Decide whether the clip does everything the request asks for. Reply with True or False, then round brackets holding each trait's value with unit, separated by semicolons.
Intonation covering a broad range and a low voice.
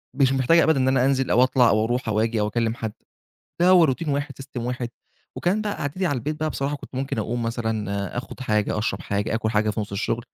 False (4.1 semitones; 125 Hz)